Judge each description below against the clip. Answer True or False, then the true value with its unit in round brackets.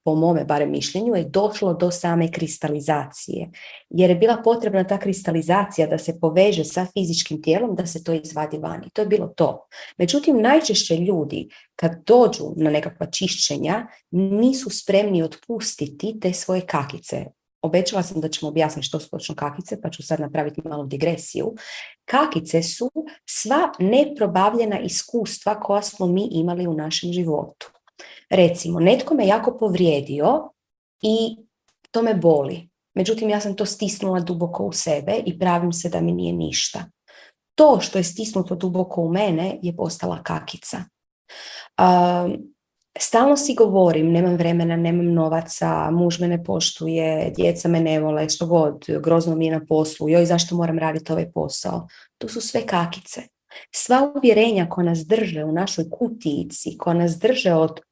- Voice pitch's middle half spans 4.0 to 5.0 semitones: True (4.3 semitones)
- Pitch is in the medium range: True (175 Hz)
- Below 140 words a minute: False (155 wpm)